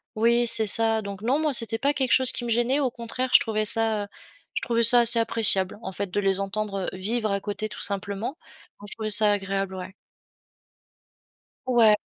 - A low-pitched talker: No, high, 220 Hz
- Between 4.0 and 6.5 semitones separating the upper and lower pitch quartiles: No, average, 2.9 semitones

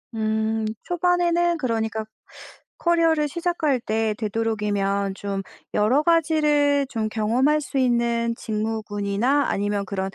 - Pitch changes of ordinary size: No, wide, 5.8 semitones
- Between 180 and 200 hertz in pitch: No, high, 230 Hz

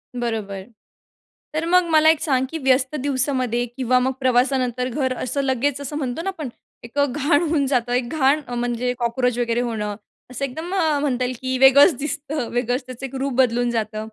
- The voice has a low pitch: No, very high, 255 Hz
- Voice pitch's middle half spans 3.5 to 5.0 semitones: No, average, 2.8 semitones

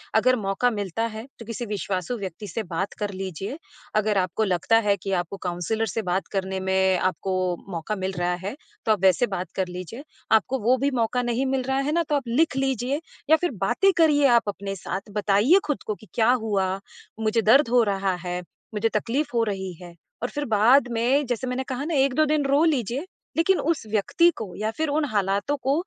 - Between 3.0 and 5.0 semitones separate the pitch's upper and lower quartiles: No, wide, 5.6 semitones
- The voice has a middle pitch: No, high, 220 Hz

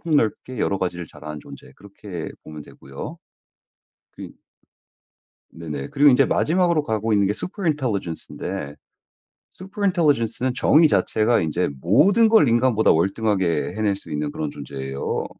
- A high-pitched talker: No, low, 110 Hz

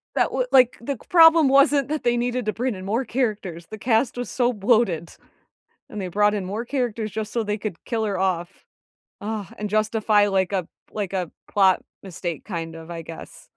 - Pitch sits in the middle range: No, high, 215 Hz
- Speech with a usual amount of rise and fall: Yes, average, 4.2 semitones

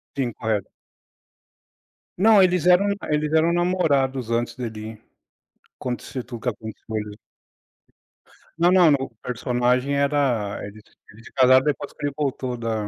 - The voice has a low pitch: Yes, low, 130 Hz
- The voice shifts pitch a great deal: No, average, 4.7 semitones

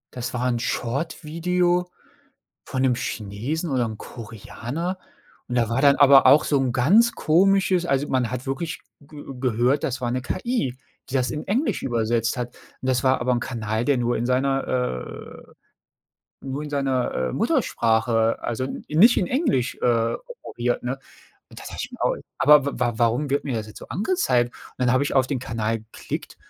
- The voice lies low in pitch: Yes, low, 130 Hz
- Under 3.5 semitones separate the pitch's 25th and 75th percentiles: No, average, 3.8 semitones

